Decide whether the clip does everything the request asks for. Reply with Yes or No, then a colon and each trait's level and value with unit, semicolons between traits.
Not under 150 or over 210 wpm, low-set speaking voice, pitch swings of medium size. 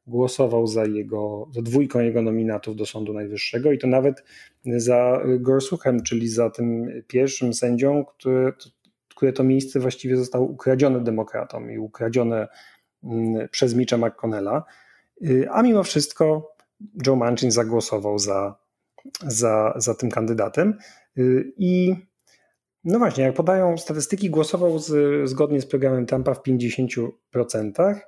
No: average, 125 wpm; low, 125 Hz; average, 3.5 semitones